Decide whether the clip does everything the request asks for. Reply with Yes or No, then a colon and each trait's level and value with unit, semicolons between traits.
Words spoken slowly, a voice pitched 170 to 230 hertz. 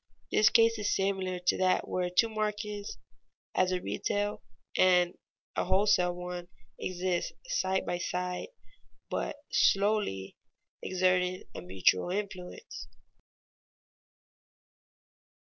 Yes: slow, 100 wpm; medium, 185 Hz